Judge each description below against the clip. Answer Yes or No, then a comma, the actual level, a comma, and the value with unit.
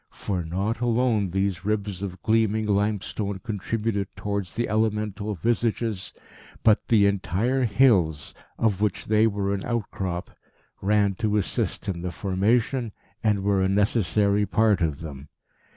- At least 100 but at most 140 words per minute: Yes, slow, 135 wpm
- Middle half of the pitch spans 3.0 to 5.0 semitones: No, narrow, 2.4 semitones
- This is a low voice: Yes, low, 100 Hz